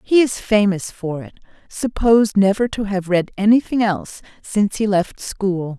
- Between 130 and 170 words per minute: Yes, average, 155 wpm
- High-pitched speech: Yes, high, 205 Hz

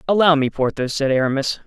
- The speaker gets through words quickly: No, average, 180 wpm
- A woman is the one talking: No, male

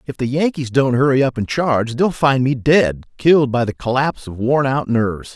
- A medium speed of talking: No, fast, 225 wpm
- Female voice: No, male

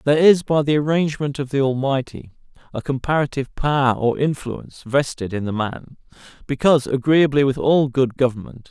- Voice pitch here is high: No, low, 135 Hz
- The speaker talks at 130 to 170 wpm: Yes, average, 160 wpm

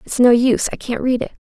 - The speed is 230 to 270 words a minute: Yes, fast, 250 wpm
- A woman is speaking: Yes, female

